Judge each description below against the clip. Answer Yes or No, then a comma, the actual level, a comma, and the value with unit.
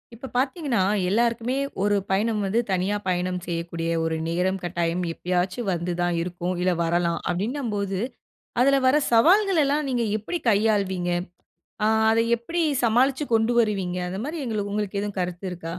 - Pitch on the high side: Yes, high, 200 Hz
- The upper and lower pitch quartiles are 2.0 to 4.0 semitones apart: No, average, 4.8 semitones